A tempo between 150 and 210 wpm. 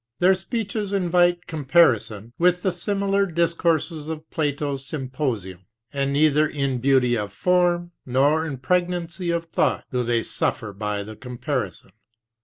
No: slow, 135 wpm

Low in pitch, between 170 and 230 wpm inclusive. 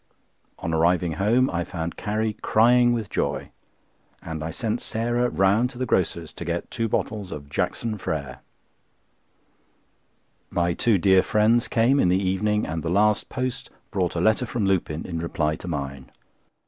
No: very low, 95 Hz; average, 160 wpm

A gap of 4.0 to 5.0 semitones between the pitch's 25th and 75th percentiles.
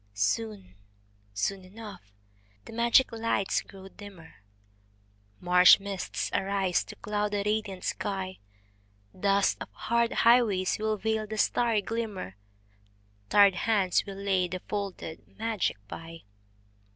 No: average, 2.8 semitones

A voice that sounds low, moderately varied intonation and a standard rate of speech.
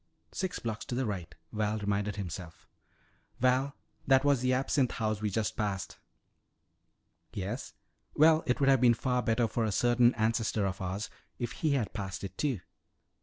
Yes: low, 115 Hz; average, 3.9 semitones; average, 165 wpm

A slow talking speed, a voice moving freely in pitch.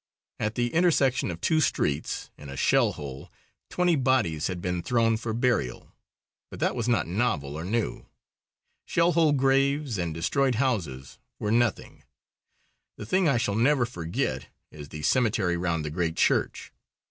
No: average, 160 wpm; wide, 8.0 semitones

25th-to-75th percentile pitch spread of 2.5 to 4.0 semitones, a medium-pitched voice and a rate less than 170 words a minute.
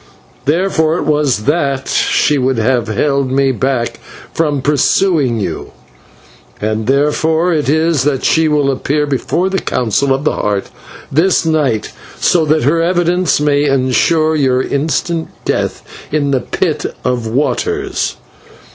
Yes: average, 3.4 semitones; medium, 145 Hz; average, 140 wpm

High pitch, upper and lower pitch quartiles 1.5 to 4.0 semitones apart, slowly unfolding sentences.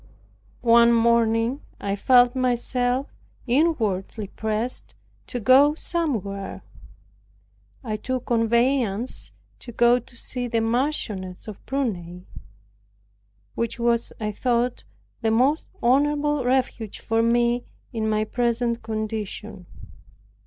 Yes: high, 235 Hz; narrow, 2.6 semitones; slow, 105 wpm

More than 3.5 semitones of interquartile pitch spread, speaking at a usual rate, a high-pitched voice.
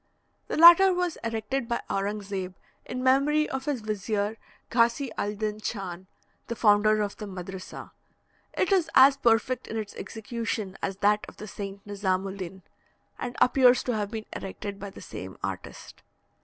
Yes: average, 4.0 semitones; average, 170 wpm; high, 215 Hz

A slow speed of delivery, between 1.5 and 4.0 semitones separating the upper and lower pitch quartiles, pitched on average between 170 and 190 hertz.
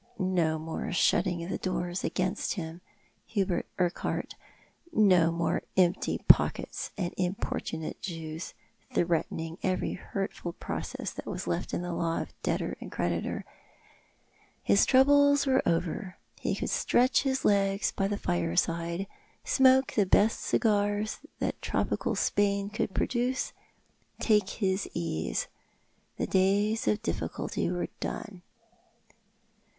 Yes: slow, 120 wpm; average, 3.5 semitones; medium, 185 Hz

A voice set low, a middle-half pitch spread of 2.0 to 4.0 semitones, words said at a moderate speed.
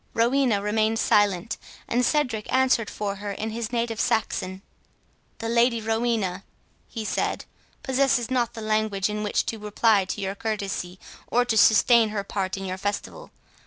No: high, 220 Hz; narrow, 2.6 semitones; average, 160 wpm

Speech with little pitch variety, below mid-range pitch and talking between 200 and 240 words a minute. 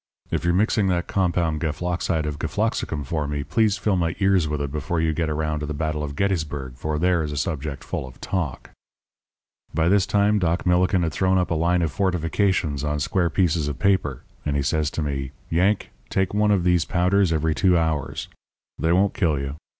No: average, 3.6 semitones; very low, 80 Hz; fast, 205 wpm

